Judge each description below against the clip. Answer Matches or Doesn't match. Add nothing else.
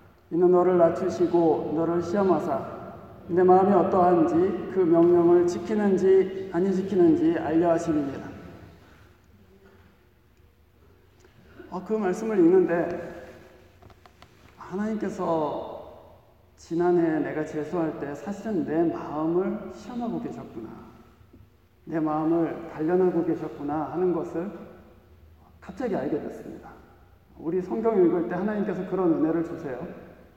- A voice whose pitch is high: Doesn't match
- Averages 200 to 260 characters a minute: Matches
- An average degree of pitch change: Doesn't match